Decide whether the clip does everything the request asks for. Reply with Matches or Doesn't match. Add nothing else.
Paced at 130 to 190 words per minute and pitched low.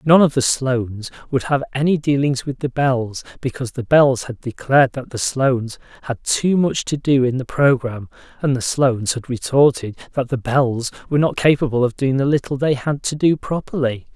Doesn't match